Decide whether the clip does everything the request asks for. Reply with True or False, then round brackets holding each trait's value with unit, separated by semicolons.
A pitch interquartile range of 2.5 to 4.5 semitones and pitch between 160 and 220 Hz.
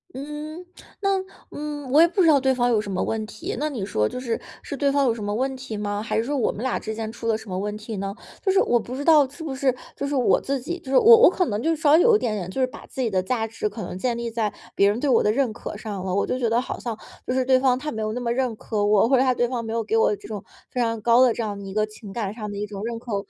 False (4.1 semitones; 235 Hz)